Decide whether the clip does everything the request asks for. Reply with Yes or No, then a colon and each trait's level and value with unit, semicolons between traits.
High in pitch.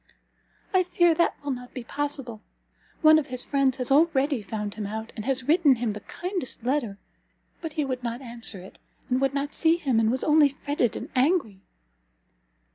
Yes: very high, 265 Hz